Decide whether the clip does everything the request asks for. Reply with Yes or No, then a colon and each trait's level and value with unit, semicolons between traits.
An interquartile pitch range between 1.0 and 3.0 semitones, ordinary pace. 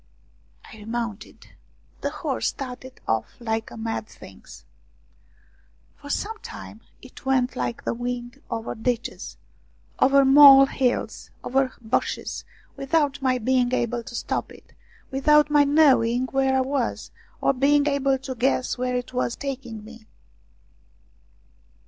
No: narrow, 2.5 semitones; slow, 130 wpm